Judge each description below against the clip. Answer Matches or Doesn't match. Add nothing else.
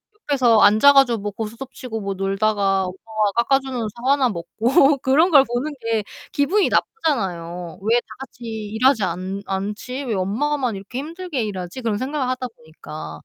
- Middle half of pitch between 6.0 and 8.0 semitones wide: Doesn't match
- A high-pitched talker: Matches